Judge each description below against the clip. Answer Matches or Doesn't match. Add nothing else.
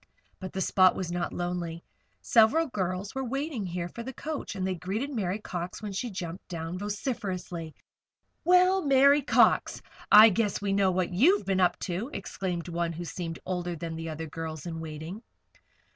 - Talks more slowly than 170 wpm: Doesn't match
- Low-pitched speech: Doesn't match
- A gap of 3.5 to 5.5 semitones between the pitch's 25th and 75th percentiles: Matches